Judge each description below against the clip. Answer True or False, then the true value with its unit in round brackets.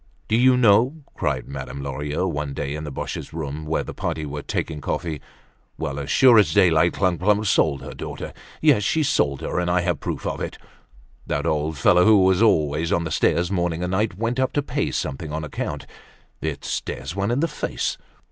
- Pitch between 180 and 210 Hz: False (85 Hz)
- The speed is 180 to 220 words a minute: True (205 wpm)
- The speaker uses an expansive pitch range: True (5.7 semitones)